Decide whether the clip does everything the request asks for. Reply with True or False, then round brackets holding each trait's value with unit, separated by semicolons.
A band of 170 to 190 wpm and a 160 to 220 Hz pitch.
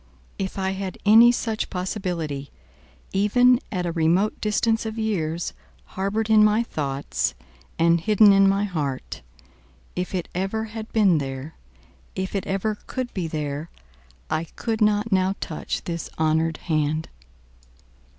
False (140 wpm; 190 Hz)